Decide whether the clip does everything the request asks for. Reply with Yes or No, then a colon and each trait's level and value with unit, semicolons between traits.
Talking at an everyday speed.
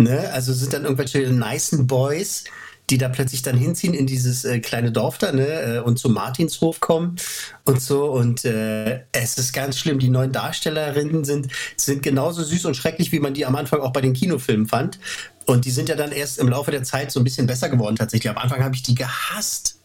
No: fast, 220 wpm